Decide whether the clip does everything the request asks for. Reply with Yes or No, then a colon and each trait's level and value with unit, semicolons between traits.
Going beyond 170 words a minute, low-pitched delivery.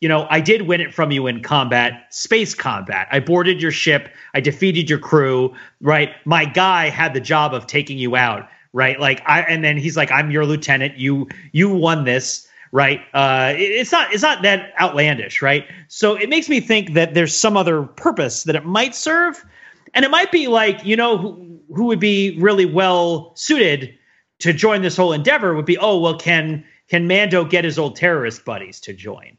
No: fast, 205 wpm; medium, 165 Hz